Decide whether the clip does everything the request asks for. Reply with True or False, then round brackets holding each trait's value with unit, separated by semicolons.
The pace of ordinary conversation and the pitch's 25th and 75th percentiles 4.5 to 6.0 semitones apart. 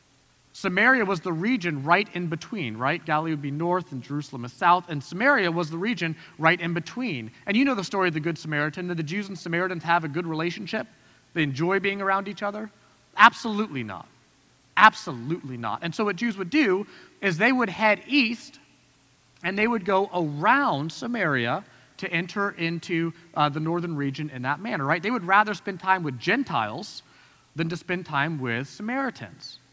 True (190 wpm; 4.8 semitones)